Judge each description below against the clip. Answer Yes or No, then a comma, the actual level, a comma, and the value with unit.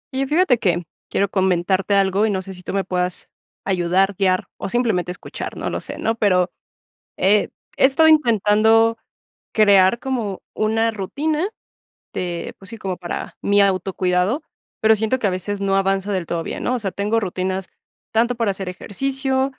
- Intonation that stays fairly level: No, average, 3.4 semitones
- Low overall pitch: No, high, 200 Hz